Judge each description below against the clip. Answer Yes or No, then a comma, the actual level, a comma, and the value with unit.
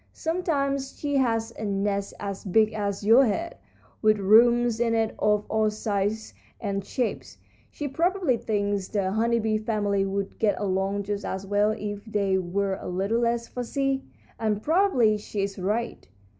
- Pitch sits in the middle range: No, high, 215 Hz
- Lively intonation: No, average, 2.8 semitones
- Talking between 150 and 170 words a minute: Yes, average, 160 wpm